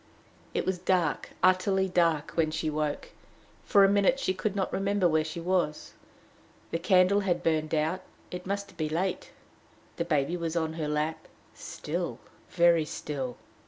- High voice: No, medium, 170 Hz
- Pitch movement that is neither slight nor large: Yes, average, 3.2 semitones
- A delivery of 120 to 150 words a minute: No, average, 160 wpm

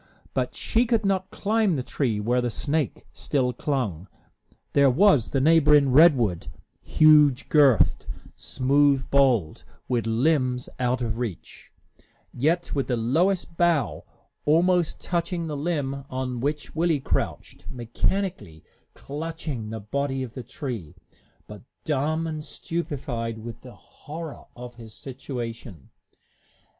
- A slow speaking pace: Yes, slow, 125 wpm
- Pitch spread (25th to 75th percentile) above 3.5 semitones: Yes, average, 4.8 semitones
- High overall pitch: No, medium, 140 Hz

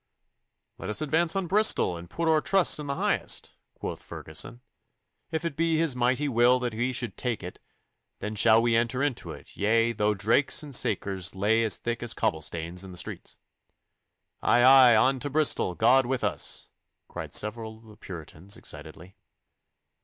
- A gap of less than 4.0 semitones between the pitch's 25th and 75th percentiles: No, average, 4.8 semitones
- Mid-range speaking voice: No, low, 120 Hz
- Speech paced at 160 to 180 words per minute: Yes, average, 175 wpm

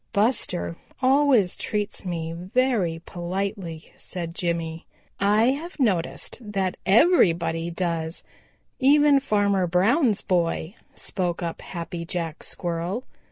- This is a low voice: No, medium, 185 Hz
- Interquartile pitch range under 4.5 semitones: No, average, 4.8 semitones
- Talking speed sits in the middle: No, slow, 105 wpm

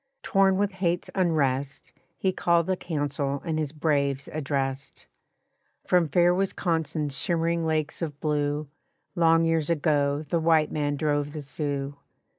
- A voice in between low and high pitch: Yes, medium, 155 Hz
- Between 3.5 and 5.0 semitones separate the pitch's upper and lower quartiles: No, average, 2.7 semitones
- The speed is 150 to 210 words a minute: No, slow, 135 wpm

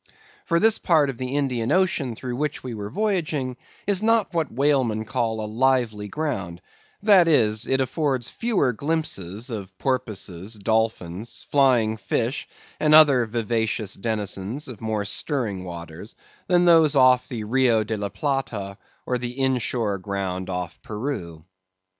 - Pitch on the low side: Yes, low, 120 Hz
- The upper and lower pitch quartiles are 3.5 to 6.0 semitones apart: Yes, average, 5.2 semitones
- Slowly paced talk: No, average, 150 wpm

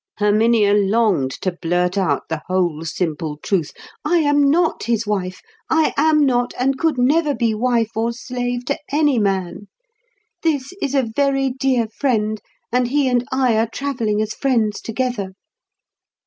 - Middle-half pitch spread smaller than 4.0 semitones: No, average, 4.8 semitones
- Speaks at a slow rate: No, average, 155 wpm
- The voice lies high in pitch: Yes, high, 235 Hz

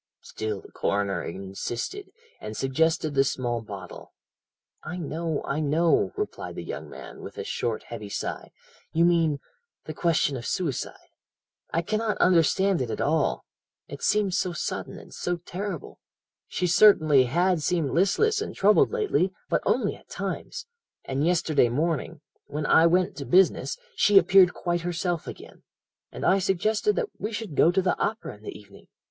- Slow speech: No, average, 165 wpm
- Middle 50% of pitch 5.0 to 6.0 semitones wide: Yes, wide, 5.5 semitones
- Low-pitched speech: No, medium, 170 Hz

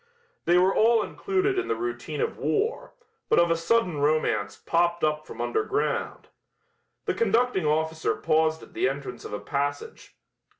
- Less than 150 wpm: No, average, 160 wpm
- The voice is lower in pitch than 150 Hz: No, medium, 165 Hz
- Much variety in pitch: Yes, wide, 7.8 semitones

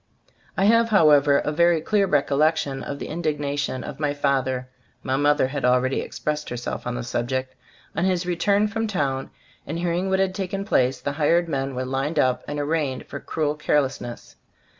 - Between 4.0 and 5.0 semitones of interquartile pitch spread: Yes, average, 4.3 semitones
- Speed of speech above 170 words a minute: Yes, average, 185 wpm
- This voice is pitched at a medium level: Yes, medium, 145 Hz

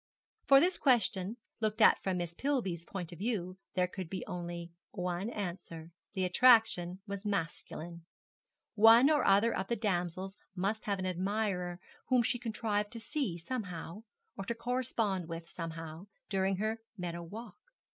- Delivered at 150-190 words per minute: Yes, average, 155 wpm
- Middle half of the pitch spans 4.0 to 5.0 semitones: Yes, average, 4.3 semitones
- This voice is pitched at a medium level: No, high, 195 Hz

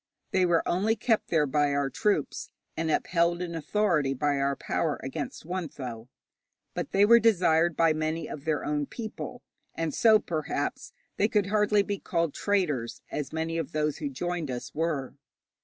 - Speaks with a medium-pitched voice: Yes, medium, 165 Hz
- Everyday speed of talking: Yes, average, 170 wpm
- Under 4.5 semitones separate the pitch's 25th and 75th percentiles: No, average, 5.1 semitones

